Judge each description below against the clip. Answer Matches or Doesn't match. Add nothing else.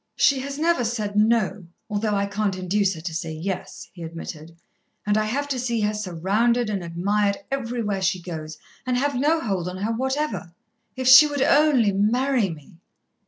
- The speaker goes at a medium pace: Matches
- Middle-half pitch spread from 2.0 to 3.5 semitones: Doesn't match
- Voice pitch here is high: Matches